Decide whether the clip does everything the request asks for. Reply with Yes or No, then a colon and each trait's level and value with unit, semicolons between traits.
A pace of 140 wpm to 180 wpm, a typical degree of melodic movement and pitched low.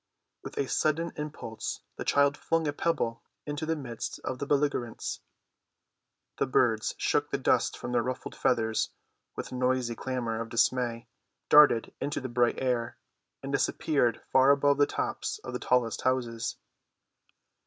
Yes: average, 150 wpm; average, 3.4 semitones; low, 130 Hz